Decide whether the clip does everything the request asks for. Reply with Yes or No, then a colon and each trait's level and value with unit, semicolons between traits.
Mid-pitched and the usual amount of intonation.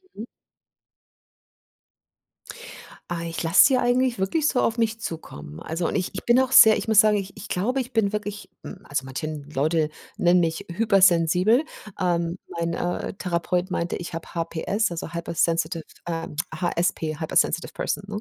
Yes: medium, 175 Hz; average, 4.4 semitones